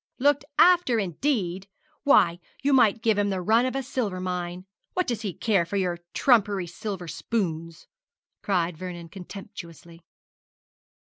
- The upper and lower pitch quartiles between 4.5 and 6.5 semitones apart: Yes, average, 5.0 semitones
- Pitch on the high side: Yes, high, 195 Hz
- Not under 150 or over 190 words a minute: No, average, 140 wpm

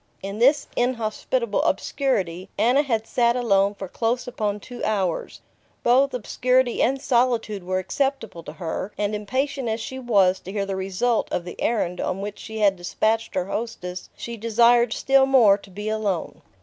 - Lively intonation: No, average, 3.9 semitones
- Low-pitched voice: No, high, 220 Hz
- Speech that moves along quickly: No, average, 170 wpm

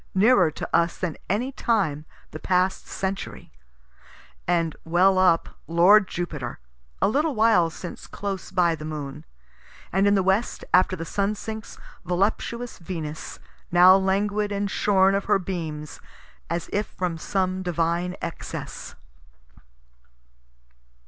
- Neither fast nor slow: No, slow, 130 wpm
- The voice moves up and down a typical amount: Yes, average, 3.1 semitones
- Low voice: No, medium, 185 Hz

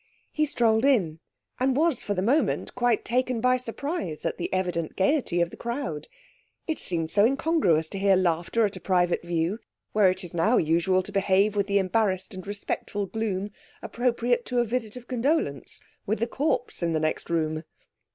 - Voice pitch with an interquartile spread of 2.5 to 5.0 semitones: No, wide, 5.6 semitones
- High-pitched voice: Yes, high, 205 Hz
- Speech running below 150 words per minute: No, average, 185 wpm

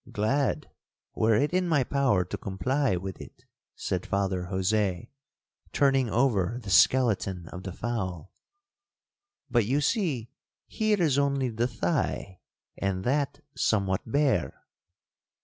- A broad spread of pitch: Yes, wide, 6.4 semitones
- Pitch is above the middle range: No, low, 115 Hz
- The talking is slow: Yes, slow, 125 wpm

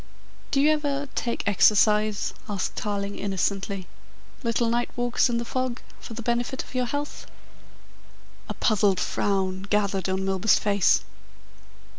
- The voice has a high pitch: Yes, high, 215 Hz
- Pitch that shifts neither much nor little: Yes, average, 3.5 semitones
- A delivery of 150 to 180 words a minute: No, slow, 135 wpm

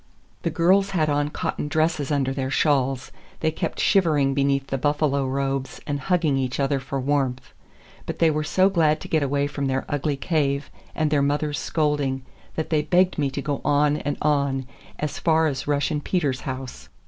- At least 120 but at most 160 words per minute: No, average, 185 wpm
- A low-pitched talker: No, medium, 145 Hz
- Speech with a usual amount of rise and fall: No, narrow, 2.1 semitones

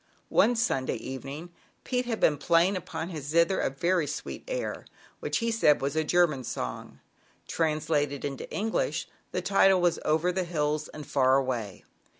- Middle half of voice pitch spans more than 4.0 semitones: Yes, average, 4.4 semitones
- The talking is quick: No, average, 160 wpm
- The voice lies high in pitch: No, medium, 160 Hz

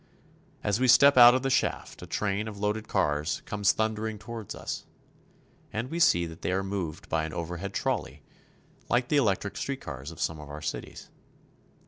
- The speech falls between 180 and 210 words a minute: Yes, average, 185 wpm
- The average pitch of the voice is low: Yes, low, 100 Hz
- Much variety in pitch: Yes, wide, 6.0 semitones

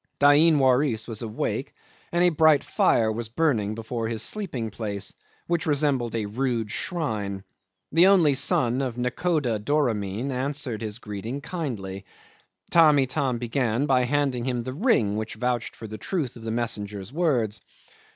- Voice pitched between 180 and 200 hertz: No, low, 125 Hz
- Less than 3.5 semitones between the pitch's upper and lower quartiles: No, average, 4.7 semitones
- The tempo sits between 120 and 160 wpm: Yes, average, 150 wpm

